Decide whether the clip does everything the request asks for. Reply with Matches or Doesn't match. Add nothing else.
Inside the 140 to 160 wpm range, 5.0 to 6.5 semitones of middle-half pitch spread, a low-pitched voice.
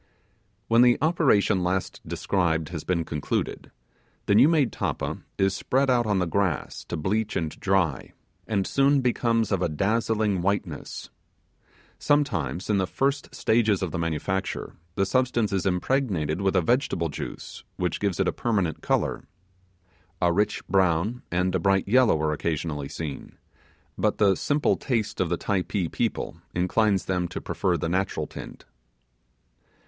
Doesn't match